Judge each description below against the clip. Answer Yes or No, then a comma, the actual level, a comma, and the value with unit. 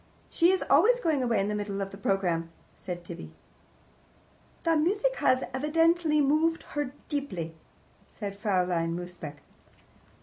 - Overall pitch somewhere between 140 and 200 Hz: No, high, 230 Hz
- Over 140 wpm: No, slow, 135 wpm